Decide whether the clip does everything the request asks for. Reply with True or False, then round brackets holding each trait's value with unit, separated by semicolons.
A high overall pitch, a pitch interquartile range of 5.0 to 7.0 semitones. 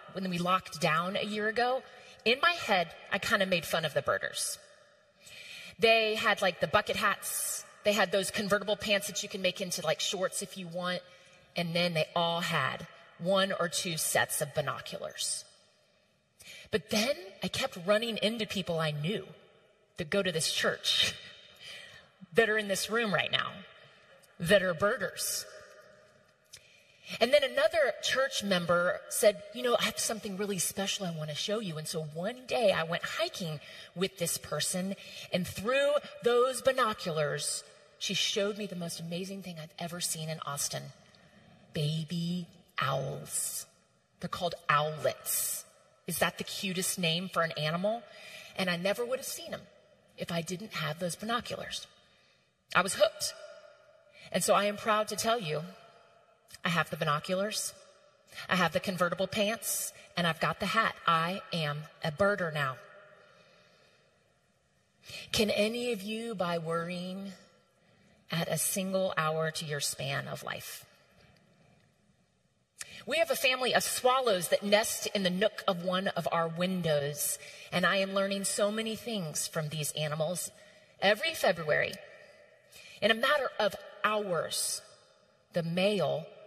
False (195 Hz; 3.7 semitones)